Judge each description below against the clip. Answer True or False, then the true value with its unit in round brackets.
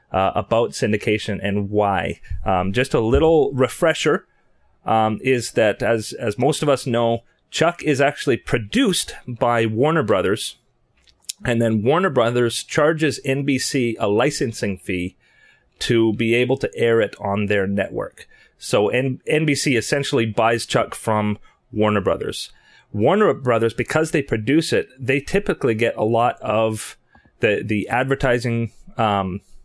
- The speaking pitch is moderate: False (115 Hz)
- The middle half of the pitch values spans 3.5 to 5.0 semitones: True (4.1 semitones)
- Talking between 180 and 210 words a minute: False (140 wpm)